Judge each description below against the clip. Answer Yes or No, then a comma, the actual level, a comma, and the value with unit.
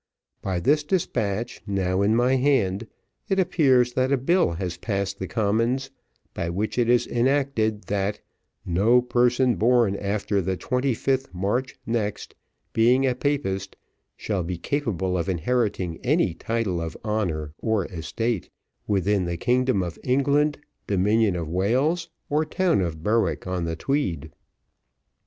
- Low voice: Yes, low, 110 Hz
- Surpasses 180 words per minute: No, average, 140 wpm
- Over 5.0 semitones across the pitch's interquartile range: Yes, wide, 5.4 semitones